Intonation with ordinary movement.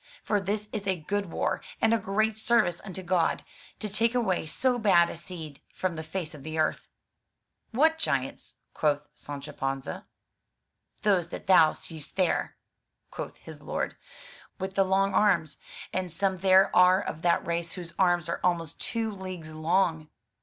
Yes: average, 3.7 semitones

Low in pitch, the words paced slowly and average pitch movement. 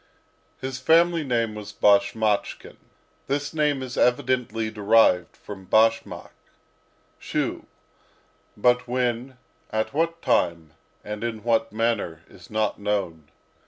Yes: low, 115 Hz; slow, 110 wpm; average, 3.6 semitones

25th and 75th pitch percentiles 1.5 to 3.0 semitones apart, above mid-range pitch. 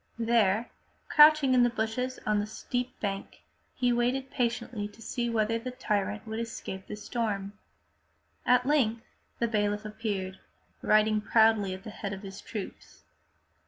Yes: average, 2.7 semitones; high, 220 Hz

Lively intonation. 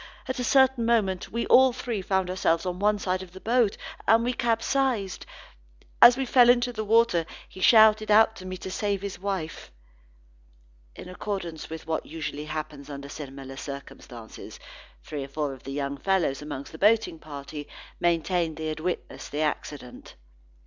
Yes: wide, 6.5 semitones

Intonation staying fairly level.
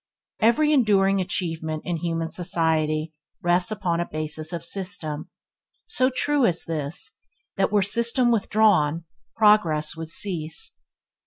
No: average, 4.9 semitones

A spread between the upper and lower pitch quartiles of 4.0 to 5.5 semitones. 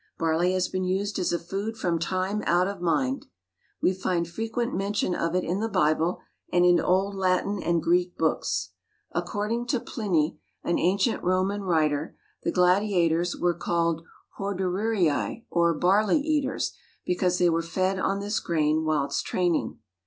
No: average, 2.9 semitones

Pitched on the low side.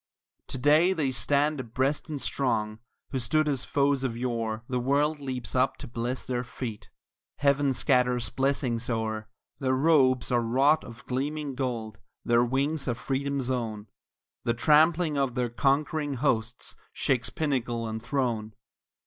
Yes: low, 130 Hz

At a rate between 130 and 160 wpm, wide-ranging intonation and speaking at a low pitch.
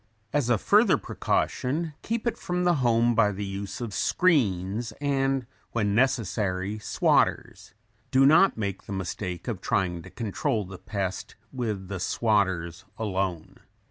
Yes: average, 140 wpm; wide, 5.7 semitones; low, 110 Hz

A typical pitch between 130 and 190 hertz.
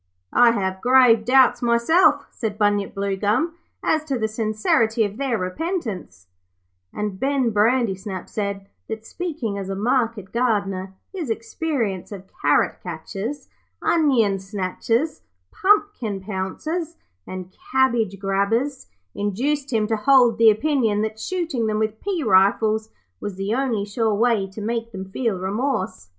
No: high, 220 Hz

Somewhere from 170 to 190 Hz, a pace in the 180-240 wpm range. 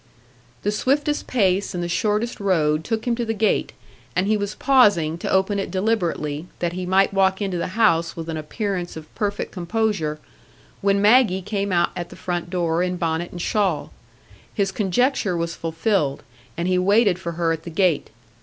Yes: medium, 185 Hz; average, 185 wpm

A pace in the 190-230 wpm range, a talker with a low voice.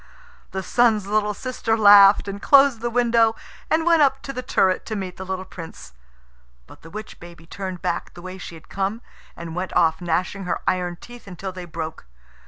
No: average, 195 wpm; high, 195 Hz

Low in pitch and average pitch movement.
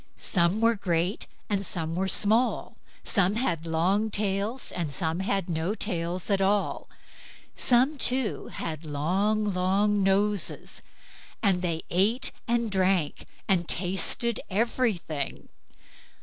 No: high, 195 Hz; average, 3.6 semitones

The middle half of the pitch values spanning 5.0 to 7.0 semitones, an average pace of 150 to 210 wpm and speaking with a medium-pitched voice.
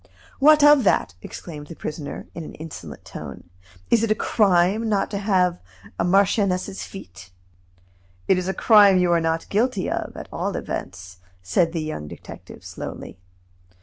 No: average, 4.6 semitones; average, 160 wpm; medium, 180 Hz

